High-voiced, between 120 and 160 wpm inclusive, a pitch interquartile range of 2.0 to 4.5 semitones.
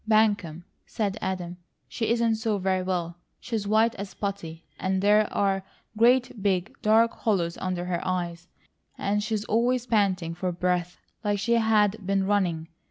Yes: high, 200 Hz; average, 155 wpm; average, 3.3 semitones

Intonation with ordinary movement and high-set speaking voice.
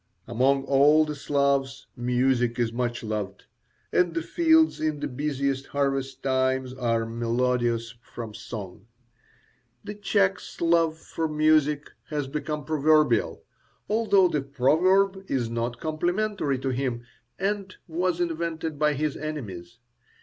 No: average, 4.5 semitones; medium, 140 Hz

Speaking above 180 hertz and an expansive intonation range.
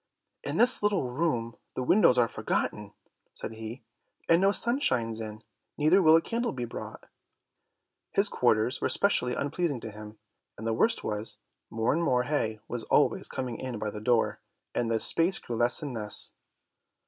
No: low, 125 Hz; wide, 6.6 semitones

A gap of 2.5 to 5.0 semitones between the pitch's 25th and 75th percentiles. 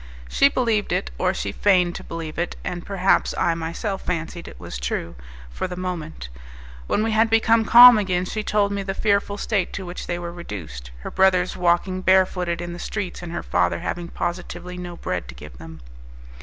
Yes: average, 3.1 semitones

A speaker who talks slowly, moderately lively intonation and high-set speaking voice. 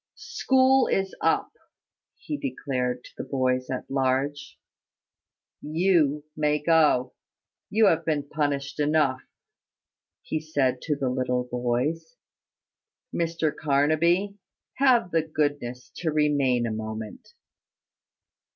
No: slow, 105 wpm; average, 4.2 semitones; medium, 145 Hz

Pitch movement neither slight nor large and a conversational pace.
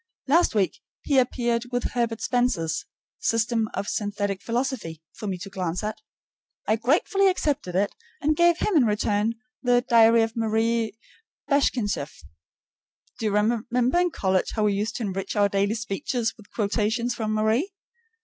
Yes: average, 3.1 semitones; average, 155 wpm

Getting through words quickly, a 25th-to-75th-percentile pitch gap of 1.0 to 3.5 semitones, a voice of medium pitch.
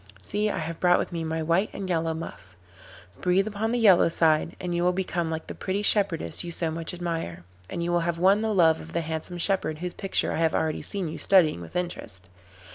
Yes: fast, 230 wpm; average, 2.7 semitones; medium, 170 Hz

